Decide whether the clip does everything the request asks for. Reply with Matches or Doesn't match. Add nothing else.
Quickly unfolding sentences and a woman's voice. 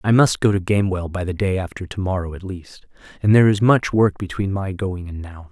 Doesn't match